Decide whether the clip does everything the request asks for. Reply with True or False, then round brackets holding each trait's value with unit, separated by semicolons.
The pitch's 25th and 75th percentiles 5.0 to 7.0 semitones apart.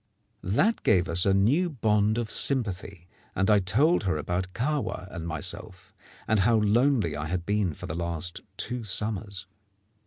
False (4.3 semitones)